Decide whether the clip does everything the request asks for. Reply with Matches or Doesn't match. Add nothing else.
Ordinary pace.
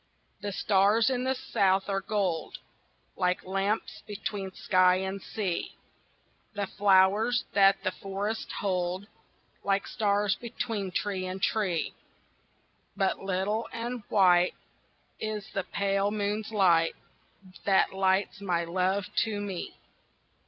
Doesn't match